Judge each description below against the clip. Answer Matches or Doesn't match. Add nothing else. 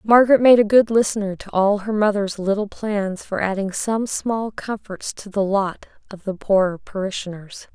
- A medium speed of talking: Matches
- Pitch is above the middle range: Matches